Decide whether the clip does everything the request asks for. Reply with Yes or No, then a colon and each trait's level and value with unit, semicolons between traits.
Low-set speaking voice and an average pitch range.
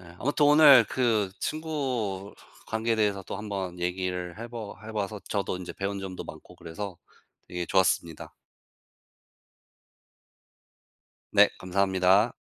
Yes: low, 100 Hz; average, 3.6 semitones